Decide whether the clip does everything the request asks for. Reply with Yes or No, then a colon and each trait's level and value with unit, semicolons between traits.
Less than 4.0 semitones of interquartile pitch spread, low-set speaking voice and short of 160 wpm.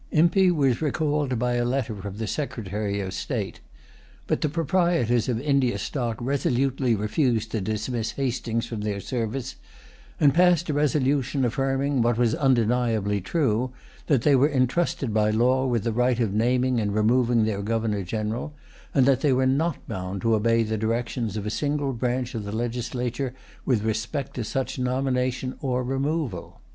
No: average, 3.5 semitones; low, 125 Hz; average, 165 wpm